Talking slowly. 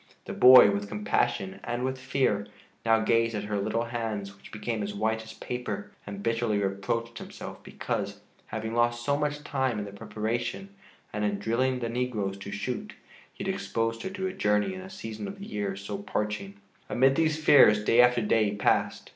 No: average, 190 wpm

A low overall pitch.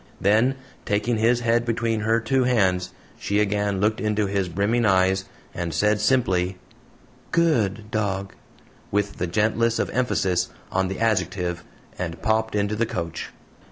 Yes: low, 105 Hz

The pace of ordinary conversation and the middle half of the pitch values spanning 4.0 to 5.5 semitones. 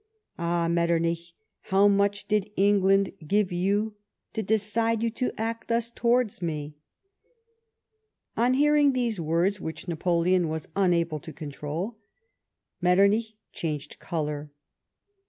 No: slow, 120 wpm; average, 4.7 semitones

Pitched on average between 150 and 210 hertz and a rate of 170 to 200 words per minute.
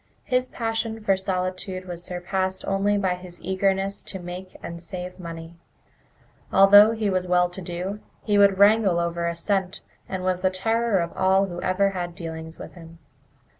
Yes: medium, 185 Hz; average, 175 wpm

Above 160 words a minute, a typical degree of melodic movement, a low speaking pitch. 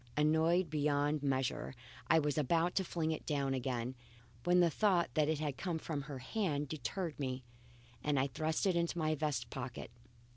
No: average, 180 wpm; average, 3.1 semitones; medium, 150 Hz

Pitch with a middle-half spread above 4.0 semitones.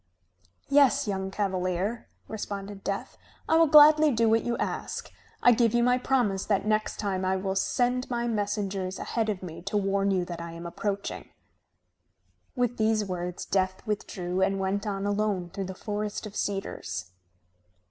No: average, 2.9 semitones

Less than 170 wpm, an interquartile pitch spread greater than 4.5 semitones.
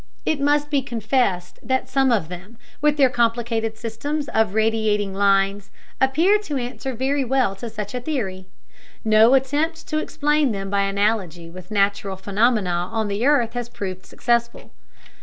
Yes: average, 160 wpm; average, 5.1 semitones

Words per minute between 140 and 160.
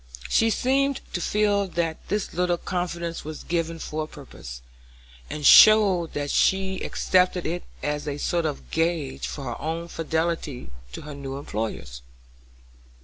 Yes: average, 145 wpm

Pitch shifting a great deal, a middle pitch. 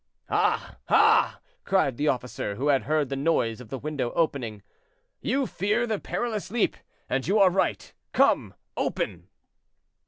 Yes: wide, 7.4 semitones; medium, 150 Hz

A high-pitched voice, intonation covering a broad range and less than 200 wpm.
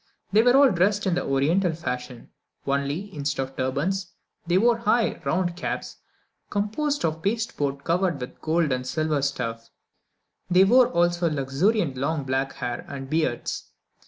No: medium, 160 Hz; wide, 6.0 semitones; average, 150 wpm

